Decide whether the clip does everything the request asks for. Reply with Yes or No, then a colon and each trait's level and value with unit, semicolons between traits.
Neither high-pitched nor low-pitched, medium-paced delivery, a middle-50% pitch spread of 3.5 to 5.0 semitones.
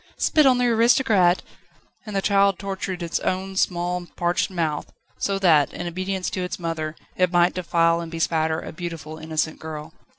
No: medium, 175 Hz; average, 170 wpm; average, 2.8 semitones